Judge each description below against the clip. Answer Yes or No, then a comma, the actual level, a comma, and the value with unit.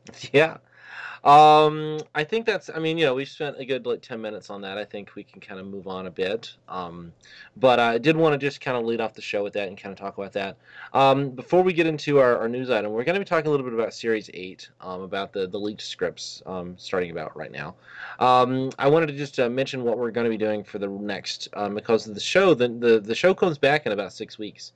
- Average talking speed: No, fast, 270 wpm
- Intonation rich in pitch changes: Yes, wide, 6.0 semitones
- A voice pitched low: Yes, low, 120 Hz